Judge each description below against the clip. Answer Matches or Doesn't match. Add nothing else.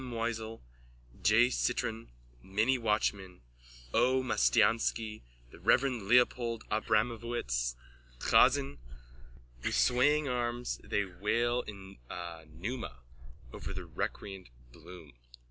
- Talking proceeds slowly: Matches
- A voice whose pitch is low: Matches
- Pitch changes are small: Doesn't match